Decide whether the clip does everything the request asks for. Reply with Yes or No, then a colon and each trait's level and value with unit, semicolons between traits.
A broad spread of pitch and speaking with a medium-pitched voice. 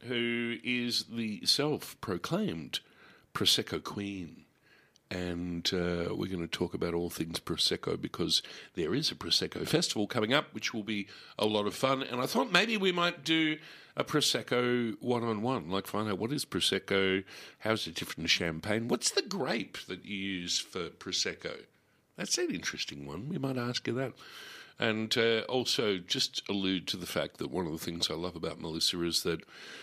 No: wide, 5.7 semitones; low, 105 Hz